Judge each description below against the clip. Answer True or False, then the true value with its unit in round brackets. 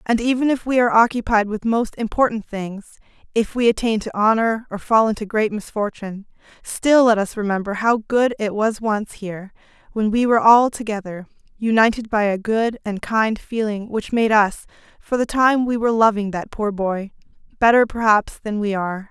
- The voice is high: True (220 Hz)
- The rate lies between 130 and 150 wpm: False (180 wpm)